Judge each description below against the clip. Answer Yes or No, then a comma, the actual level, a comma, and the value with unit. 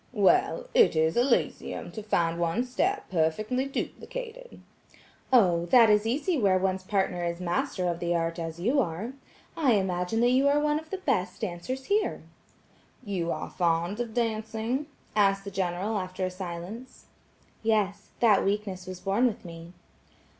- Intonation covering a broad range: Yes, wide, 5.9 semitones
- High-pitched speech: Yes, high, 205 Hz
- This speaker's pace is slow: No, average, 160 wpm